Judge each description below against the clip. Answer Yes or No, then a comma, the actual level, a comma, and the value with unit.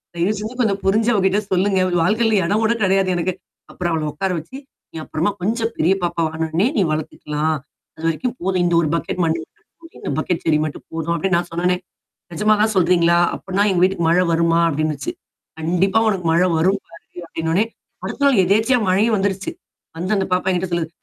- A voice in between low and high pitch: Yes, medium, 180 Hz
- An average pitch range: Yes, average, 3.4 semitones